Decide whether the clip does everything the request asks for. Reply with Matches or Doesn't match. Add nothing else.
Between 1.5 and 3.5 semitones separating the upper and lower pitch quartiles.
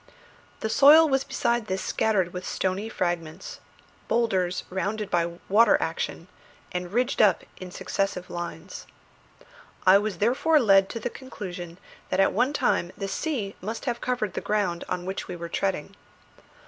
Doesn't match